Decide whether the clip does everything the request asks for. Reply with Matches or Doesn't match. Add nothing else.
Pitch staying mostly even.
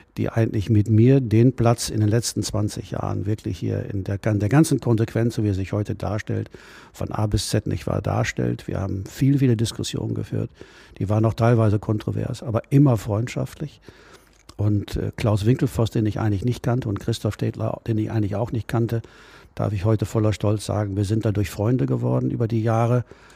Matches